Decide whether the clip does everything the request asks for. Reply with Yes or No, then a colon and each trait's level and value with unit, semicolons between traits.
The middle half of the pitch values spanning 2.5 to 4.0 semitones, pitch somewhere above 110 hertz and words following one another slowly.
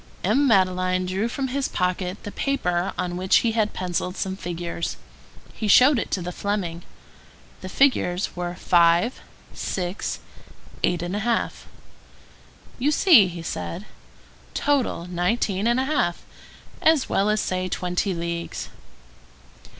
No: average, 4.4 semitones; medium, 185 Hz; slow, 125 wpm